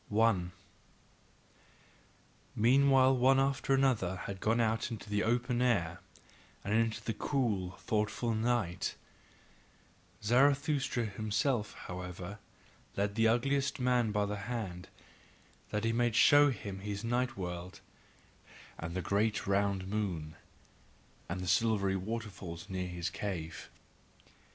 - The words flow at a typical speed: No, slow, 120 wpm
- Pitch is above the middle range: No, low, 110 Hz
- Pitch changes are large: No, average, 4.0 semitones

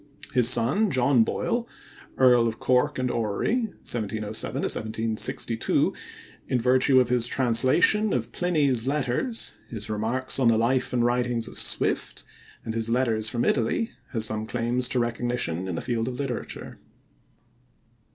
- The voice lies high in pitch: No, low, 120 Hz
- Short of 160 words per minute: Yes, average, 140 wpm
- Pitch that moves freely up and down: No, narrow, 2.4 semitones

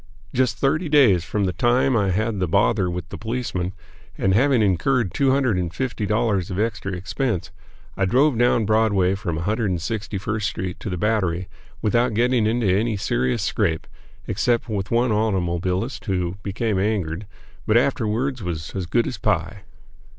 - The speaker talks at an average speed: Yes, average, 160 wpm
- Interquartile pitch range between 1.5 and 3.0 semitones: No, average, 4.2 semitones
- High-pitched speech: No, low, 105 Hz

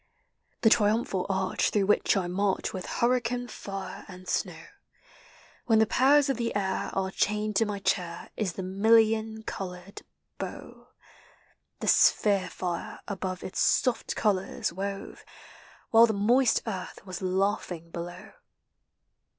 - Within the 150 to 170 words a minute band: No, slow, 135 wpm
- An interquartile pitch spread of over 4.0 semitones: No, average, 3.0 semitones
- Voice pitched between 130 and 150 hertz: No, high, 200 Hz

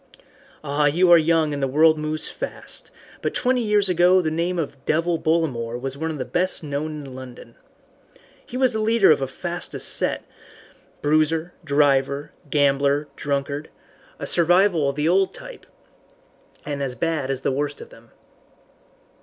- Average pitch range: Yes, average, 3.7 semitones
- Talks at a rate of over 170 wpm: No, average, 160 wpm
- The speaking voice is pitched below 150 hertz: No, medium, 155 Hz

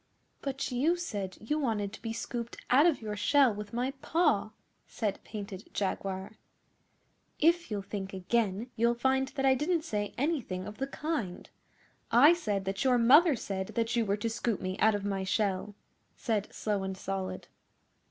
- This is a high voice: Yes, high, 225 Hz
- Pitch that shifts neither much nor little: Yes, average, 5.0 semitones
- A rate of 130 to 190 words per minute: Yes, average, 170 wpm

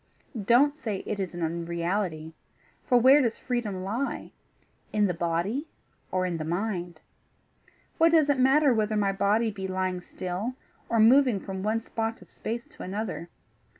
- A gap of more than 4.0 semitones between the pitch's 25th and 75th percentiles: Yes, average, 4.7 semitones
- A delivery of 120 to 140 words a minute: No, average, 160 wpm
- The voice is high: Yes, high, 210 Hz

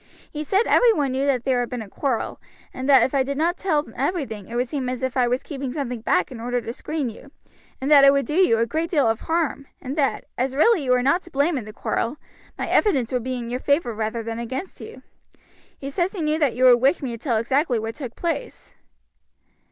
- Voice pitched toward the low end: No, very high, 265 Hz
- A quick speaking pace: Yes, fast, 245 wpm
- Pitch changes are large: No, average, 3.8 semitones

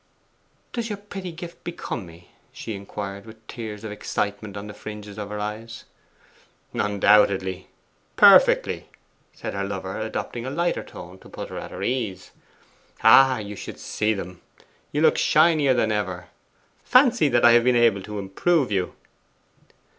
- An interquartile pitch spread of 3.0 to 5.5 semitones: Yes, average, 4.7 semitones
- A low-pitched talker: Yes, low, 105 Hz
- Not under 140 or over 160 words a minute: Yes, average, 155 wpm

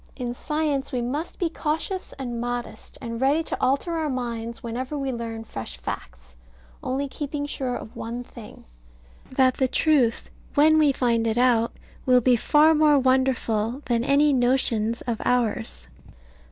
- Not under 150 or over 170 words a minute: Yes, average, 155 wpm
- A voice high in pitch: Yes, very high, 255 Hz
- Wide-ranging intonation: No, average, 3.6 semitones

